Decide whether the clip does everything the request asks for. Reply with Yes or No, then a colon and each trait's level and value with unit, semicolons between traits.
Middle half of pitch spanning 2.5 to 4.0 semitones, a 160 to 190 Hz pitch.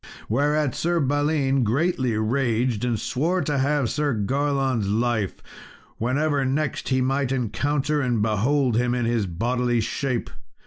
No: average, 3.6 semitones; low, 130 Hz